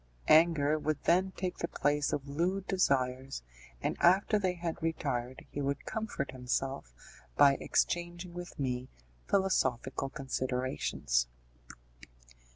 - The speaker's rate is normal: No, slow, 115 wpm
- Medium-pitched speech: Yes, medium, 145 Hz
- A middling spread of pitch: Yes, average, 4.9 semitones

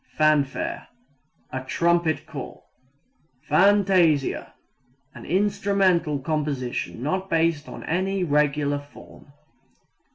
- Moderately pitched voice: Yes, medium, 160 Hz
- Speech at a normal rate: No, slow, 85 wpm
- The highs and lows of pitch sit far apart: No, average, 4.5 semitones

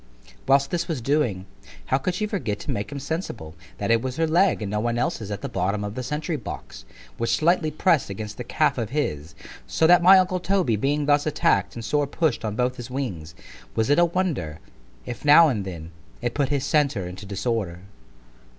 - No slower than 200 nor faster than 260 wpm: Yes, fast, 205 wpm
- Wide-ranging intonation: Yes, wide, 7.0 semitones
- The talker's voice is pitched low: Yes, low, 130 Hz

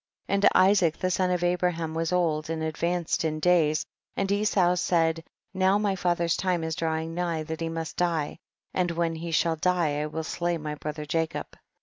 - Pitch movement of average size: No, narrow, 1.9 semitones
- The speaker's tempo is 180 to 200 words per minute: Yes, average, 190 wpm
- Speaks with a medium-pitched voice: Yes, medium, 170 Hz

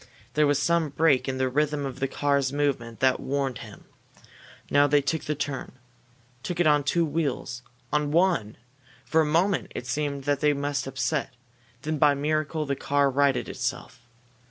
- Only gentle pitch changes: Yes, narrow, 2.0 semitones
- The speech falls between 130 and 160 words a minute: No, average, 180 wpm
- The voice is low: No, medium, 145 Hz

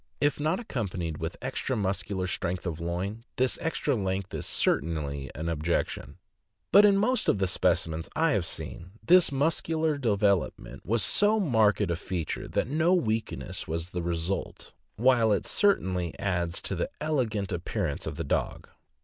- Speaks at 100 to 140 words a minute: No, average, 160 wpm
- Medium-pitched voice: No, low, 100 Hz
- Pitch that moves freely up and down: Yes, wide, 8.5 semitones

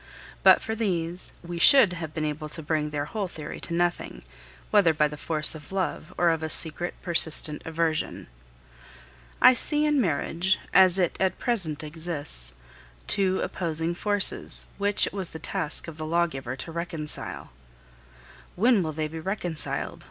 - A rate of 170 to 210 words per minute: No, average, 160 wpm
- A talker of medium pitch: Yes, medium, 170 Hz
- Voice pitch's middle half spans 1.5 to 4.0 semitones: Yes, average, 3.4 semitones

